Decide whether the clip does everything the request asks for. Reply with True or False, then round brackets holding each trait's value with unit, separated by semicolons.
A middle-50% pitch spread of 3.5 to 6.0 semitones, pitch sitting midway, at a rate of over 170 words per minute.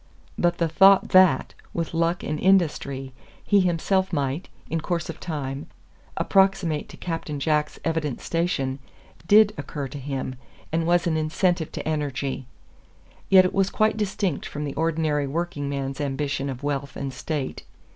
False (3.9 semitones; 155 Hz; 155 wpm)